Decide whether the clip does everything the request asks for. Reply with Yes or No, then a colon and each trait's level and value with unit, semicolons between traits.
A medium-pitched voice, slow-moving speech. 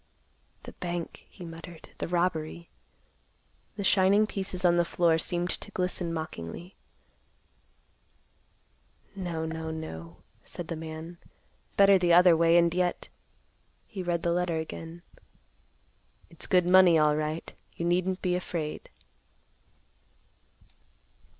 Yes: medium, 170 Hz; slow, 115 wpm